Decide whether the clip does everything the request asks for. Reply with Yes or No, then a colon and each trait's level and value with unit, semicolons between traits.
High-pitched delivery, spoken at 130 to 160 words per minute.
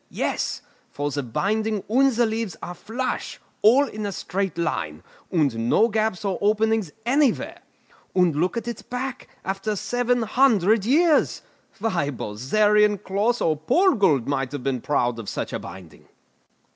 Yes: high, 205 Hz; average, 150 wpm